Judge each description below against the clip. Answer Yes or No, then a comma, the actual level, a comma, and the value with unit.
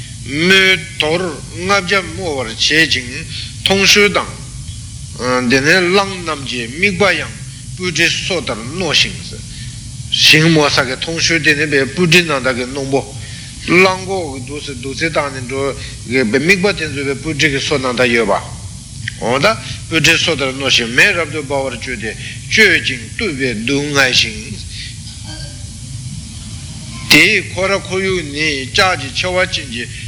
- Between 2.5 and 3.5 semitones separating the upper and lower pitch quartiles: No, average, 5.1 semitones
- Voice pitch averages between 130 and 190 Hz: Yes, low, 135 Hz